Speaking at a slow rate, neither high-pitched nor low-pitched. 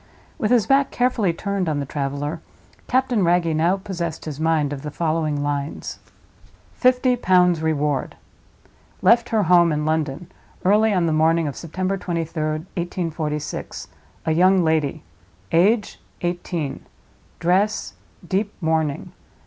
Yes: slow, 125 wpm; medium, 170 Hz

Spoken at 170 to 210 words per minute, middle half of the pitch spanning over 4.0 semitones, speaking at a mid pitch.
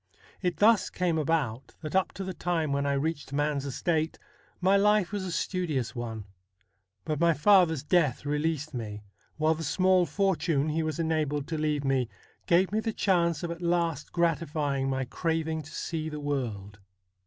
No: average, 175 wpm; average, 3.5 semitones; medium, 160 Hz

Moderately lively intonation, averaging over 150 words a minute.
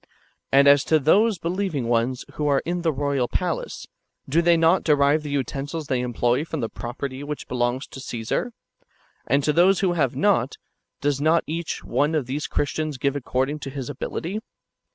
Yes: average, 3.6 semitones; average, 180 wpm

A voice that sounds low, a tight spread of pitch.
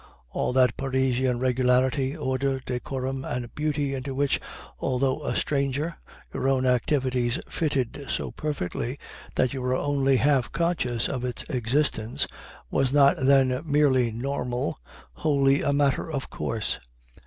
Yes: low, 130 Hz; narrow, 1.9 semitones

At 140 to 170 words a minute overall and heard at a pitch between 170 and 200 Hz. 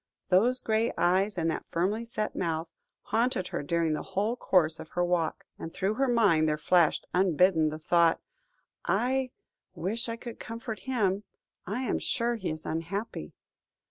Yes: average, 165 wpm; high, 190 Hz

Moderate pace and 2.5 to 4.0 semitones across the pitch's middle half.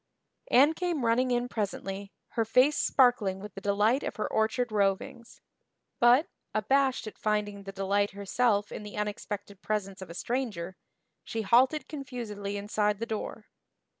Yes: average, 150 wpm; average, 3.4 semitones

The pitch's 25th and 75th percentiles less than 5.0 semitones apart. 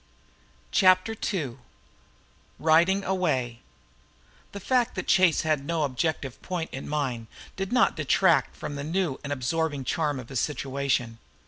No: average, 5.3 semitones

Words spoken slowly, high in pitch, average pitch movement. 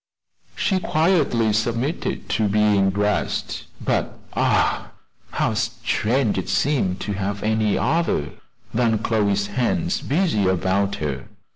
No: slow, 115 wpm; low, 110 Hz; average, 4.6 semitones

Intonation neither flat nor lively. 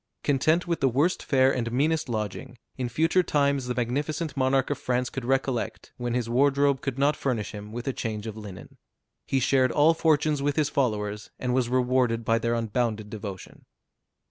Yes: average, 3.4 semitones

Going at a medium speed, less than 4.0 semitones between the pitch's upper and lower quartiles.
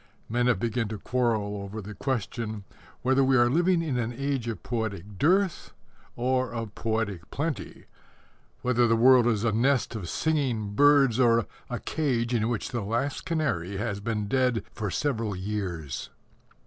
Yes: average, 160 wpm; average, 3.6 semitones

